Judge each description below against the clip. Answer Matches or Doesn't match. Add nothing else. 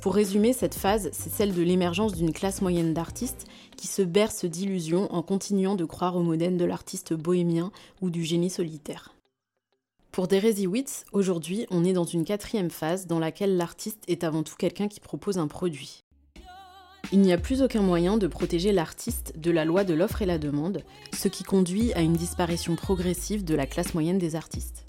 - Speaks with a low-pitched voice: Doesn't match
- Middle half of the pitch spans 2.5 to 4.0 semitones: Matches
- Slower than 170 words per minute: Doesn't match